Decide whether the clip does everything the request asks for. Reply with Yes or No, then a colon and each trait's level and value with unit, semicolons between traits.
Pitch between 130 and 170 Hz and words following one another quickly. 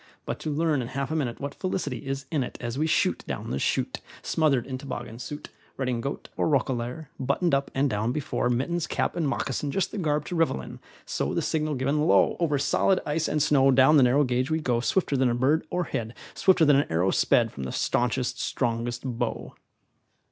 Yes: low, 135 Hz; fast, 210 wpm